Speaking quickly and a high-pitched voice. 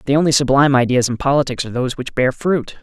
No: fast, 235 wpm; low, 135 Hz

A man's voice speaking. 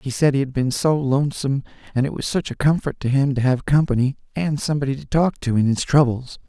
Yes: male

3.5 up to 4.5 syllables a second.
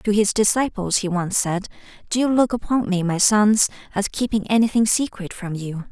No: 5.0 syllables/s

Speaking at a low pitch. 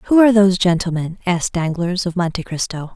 No: medium, 180 Hz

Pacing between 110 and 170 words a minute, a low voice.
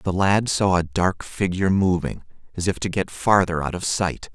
No: fast, 205 wpm; very low, 95 Hz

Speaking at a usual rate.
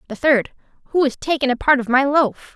No: fast, 210 wpm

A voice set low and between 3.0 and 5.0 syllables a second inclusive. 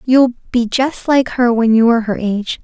No: high, 240 Hz; 4.8 syllables/s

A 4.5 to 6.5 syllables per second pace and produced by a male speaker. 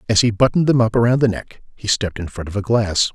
No: 6.7 syllables/s; male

